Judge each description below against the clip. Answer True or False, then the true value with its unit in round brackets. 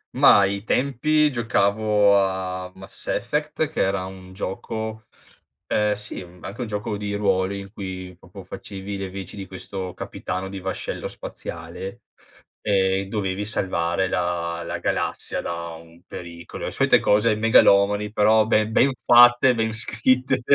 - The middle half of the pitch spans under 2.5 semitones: False (2.8 semitones)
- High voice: False (100 Hz)